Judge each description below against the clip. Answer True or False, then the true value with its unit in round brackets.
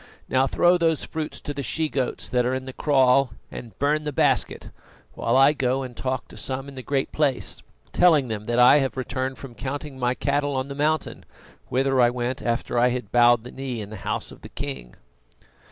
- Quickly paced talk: True (215 wpm)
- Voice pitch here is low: True (130 Hz)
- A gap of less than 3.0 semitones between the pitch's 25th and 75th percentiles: True (2.4 semitones)